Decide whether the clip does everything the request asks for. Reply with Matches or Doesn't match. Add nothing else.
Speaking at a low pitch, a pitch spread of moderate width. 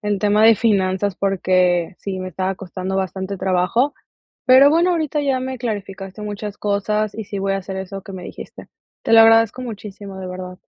Doesn't match